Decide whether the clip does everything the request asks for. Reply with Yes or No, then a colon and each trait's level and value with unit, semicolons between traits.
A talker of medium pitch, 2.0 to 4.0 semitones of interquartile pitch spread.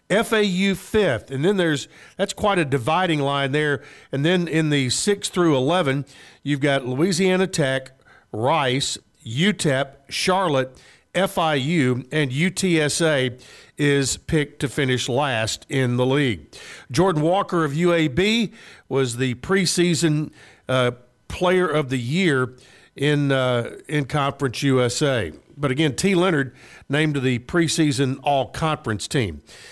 No: medium, 145 Hz; average, 4.7 semitones